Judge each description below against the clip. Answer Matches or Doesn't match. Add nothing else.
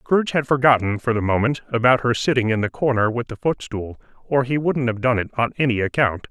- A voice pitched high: Doesn't match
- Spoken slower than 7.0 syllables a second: Matches